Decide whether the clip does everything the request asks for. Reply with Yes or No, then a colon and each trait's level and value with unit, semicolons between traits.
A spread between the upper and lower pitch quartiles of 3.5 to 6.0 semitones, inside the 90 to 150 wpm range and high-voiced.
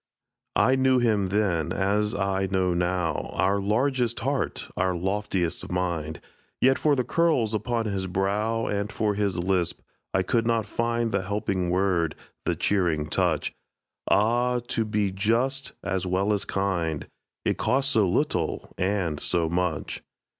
No: average, 3.9 semitones; average, 145 wpm; low, 100 Hz